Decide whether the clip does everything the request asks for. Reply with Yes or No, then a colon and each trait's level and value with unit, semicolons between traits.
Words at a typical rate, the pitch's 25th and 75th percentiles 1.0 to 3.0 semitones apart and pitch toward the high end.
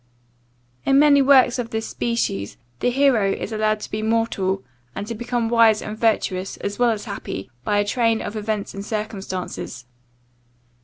Yes: average, 165 wpm; average, 2.7 semitones; high, 220 Hz